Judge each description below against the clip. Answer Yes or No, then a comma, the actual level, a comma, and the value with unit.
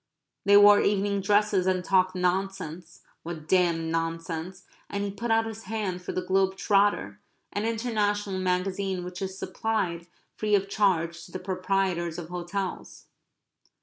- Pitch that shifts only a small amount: Yes, narrow, 2.3 semitones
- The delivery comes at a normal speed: Yes, average, 150 wpm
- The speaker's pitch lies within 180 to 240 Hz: Yes, high, 190 Hz